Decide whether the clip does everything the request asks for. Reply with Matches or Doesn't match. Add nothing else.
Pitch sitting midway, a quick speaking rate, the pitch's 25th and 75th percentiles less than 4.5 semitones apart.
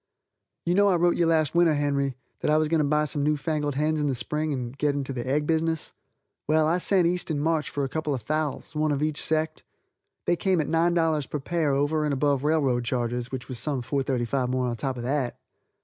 Matches